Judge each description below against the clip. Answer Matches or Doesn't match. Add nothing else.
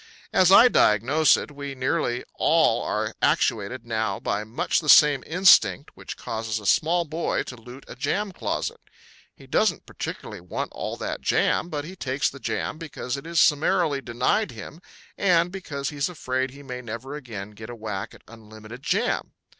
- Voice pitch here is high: Doesn't match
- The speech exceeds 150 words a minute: Matches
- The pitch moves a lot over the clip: Matches